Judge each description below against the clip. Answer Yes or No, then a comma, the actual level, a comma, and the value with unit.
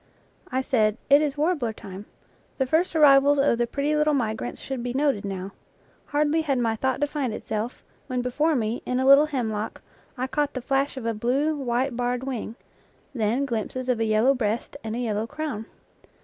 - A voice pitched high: Yes, very high, 255 Hz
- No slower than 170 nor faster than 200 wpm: Yes, average, 190 wpm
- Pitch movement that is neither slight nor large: Yes, average, 3.9 semitones